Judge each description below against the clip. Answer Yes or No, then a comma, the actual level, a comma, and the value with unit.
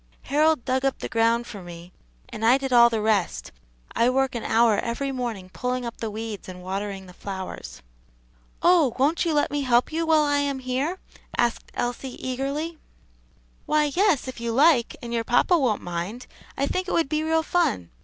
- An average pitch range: Yes, average, 4.5 semitones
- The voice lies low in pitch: No, very high, 250 Hz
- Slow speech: No, average, 195 wpm